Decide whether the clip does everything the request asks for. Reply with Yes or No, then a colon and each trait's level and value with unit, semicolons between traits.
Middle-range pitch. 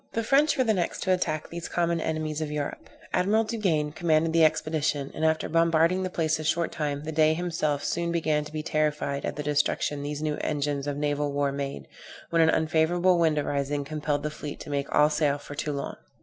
Yes: medium, 155 Hz